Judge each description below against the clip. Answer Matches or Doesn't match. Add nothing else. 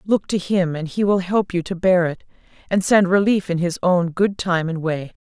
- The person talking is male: Doesn't match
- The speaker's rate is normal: Doesn't match